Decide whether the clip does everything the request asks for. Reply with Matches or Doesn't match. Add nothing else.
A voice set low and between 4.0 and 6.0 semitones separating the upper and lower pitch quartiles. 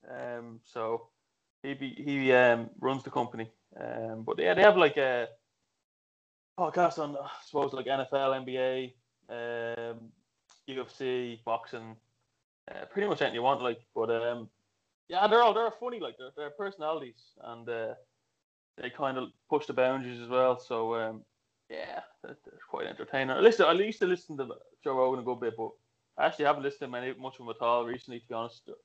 Doesn't match